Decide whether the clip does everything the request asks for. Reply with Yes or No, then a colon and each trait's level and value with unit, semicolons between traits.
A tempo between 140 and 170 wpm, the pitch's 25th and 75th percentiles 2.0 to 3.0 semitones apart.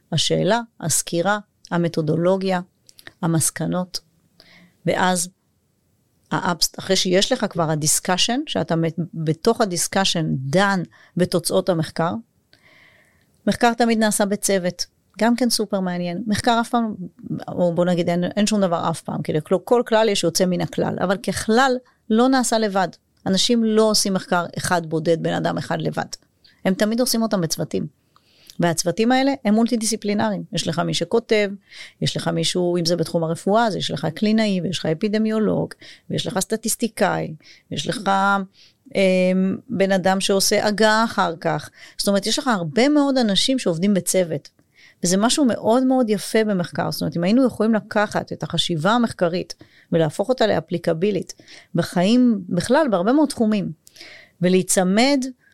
No: average, 145 wpm; average, 4.2 semitones